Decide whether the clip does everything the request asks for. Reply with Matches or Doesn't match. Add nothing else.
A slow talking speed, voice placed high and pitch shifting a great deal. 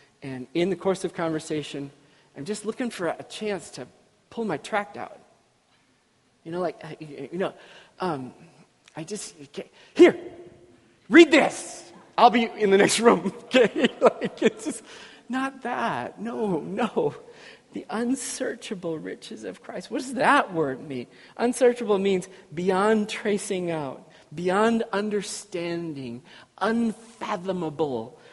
Matches